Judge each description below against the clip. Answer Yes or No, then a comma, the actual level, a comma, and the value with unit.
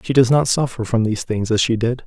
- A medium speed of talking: No, fast, 290 wpm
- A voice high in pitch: No, low, 120 Hz